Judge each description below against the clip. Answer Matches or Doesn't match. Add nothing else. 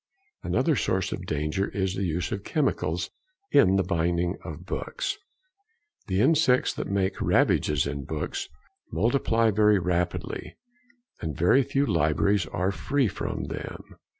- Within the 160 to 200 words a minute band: Doesn't match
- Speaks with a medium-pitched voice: Doesn't match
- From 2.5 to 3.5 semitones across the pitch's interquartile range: Doesn't match